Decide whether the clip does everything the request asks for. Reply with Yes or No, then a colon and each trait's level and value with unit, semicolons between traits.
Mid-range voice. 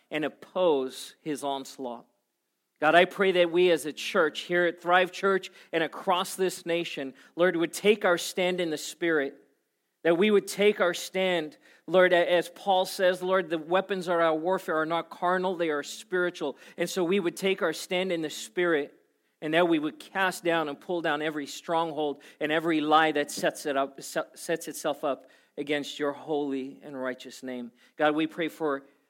Yes: medium, 170 Hz